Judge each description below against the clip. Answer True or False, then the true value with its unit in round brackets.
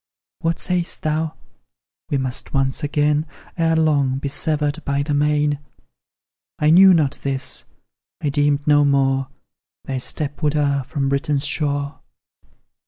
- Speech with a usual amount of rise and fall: False (1.7 semitones)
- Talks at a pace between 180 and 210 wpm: False (135 wpm)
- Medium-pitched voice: True (145 Hz)